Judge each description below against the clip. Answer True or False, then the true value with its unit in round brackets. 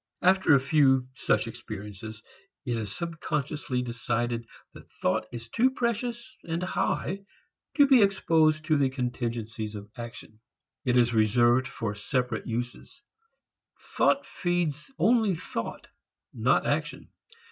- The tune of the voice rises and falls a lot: True (6.7 semitones)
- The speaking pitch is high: False (130 Hz)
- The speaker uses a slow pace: True (125 wpm)